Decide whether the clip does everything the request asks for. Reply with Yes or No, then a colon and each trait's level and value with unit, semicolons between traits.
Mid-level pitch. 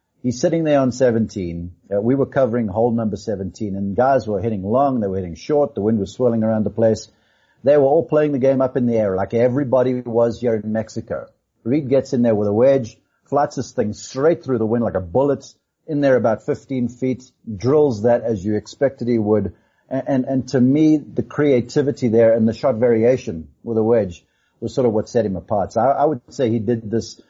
No: low, 120 Hz